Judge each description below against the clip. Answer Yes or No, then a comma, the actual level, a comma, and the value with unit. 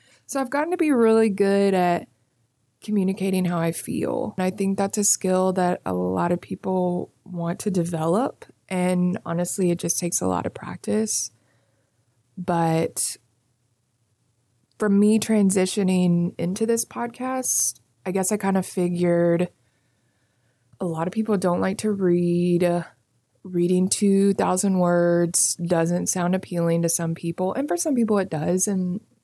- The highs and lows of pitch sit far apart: Yes, wide, 6.3 semitones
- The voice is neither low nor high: Yes, medium, 175 Hz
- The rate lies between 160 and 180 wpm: No, average, 150 wpm